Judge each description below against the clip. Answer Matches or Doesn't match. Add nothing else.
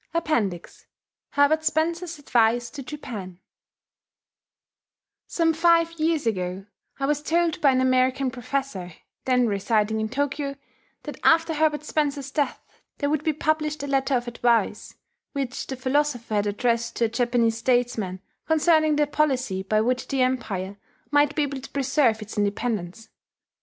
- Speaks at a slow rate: Doesn't match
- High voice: Matches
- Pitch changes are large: Doesn't match